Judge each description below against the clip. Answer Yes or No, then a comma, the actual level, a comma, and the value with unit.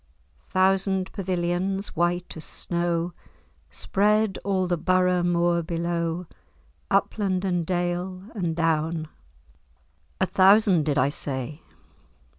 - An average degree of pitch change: No, narrow, 2.0 semitones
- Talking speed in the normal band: No, slow, 100 wpm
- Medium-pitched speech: Yes, medium, 175 Hz